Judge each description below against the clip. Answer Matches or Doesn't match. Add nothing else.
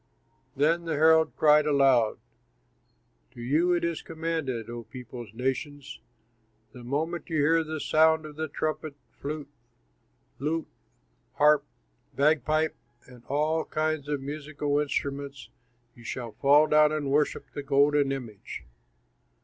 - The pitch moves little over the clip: Matches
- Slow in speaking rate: Matches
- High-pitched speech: Doesn't match